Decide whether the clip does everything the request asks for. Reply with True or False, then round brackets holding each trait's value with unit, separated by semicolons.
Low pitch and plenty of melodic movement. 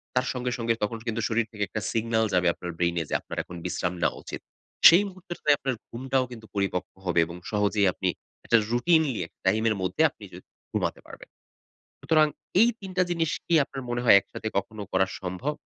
True (115 Hz; 6.0 semitones)